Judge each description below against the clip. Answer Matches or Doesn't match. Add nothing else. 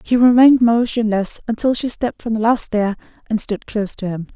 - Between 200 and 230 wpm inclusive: Matches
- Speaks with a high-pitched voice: Matches